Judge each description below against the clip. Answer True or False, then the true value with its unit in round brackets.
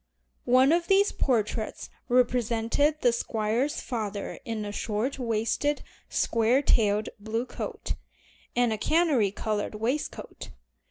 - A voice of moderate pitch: False (235 Hz)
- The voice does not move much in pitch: False (3.7 semitones)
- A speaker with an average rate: False (115 wpm)